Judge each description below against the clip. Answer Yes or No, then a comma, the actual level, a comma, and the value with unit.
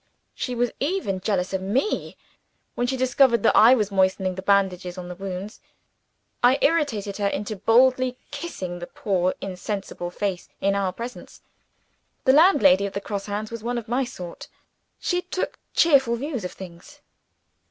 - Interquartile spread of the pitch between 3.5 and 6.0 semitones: Yes, average, 5.1 semitones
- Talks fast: No, average, 165 wpm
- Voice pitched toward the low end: No, high, 210 Hz